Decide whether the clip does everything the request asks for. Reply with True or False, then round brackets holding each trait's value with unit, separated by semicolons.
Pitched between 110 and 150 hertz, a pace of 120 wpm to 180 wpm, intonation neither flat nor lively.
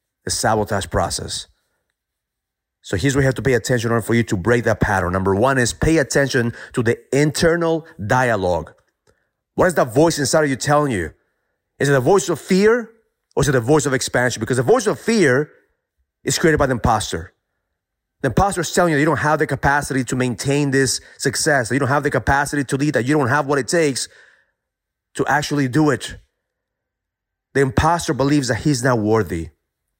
False (135 Hz; 200 wpm; 4.3 semitones)